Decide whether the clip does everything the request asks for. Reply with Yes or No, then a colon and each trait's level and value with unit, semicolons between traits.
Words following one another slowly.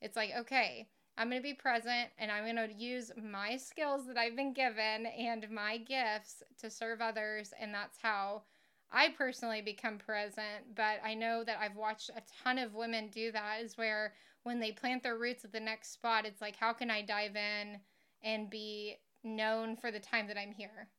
No: average, 195 wpm